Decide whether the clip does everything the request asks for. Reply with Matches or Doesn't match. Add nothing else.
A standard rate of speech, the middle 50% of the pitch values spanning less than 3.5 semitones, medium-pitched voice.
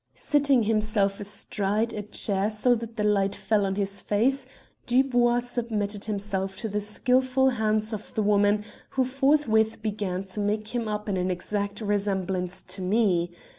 Doesn't match